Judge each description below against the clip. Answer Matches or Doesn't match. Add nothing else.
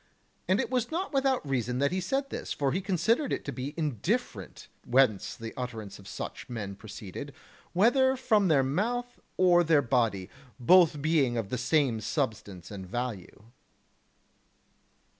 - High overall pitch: Doesn't match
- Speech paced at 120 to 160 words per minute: Matches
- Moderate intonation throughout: Doesn't match